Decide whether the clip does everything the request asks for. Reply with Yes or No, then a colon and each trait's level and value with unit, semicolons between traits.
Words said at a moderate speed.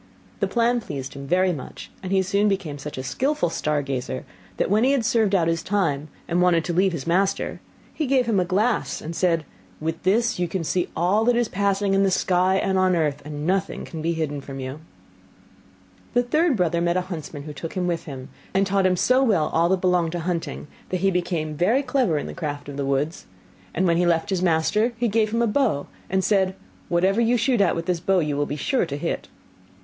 No: fast, 230 wpm